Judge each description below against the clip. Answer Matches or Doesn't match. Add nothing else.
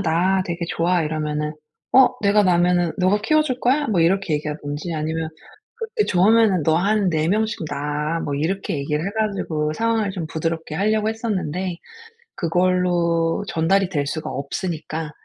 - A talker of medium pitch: Matches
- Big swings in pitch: Doesn't match